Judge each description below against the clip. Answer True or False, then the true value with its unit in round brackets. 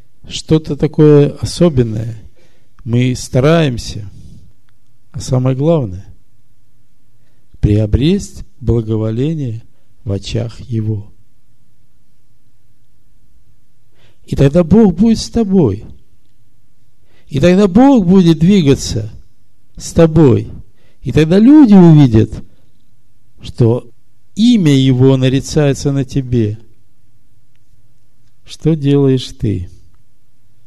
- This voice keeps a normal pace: False (75 wpm)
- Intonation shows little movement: False (3.9 semitones)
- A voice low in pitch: True (120 Hz)